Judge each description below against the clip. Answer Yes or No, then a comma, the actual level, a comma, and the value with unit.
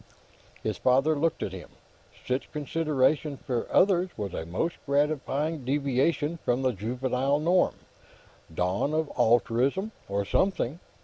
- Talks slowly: Yes, slow, 125 wpm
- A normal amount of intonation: Yes, average, 4.2 semitones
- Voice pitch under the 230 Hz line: Yes, medium, 140 Hz